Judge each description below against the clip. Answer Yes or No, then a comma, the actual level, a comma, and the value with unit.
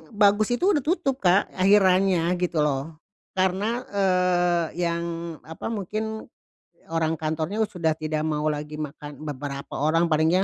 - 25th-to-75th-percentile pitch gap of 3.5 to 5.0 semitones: Yes, average, 4.3 semitones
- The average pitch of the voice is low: No, medium, 175 Hz